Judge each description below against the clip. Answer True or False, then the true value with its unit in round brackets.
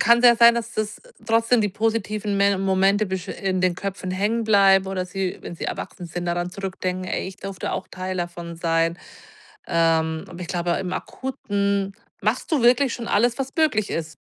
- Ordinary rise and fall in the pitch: True (3.4 semitones)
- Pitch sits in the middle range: False (195 Hz)